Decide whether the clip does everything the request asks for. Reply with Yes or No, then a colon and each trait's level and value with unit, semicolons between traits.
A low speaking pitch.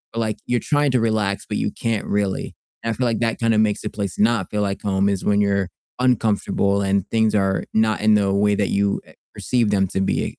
Yes: low, 105 Hz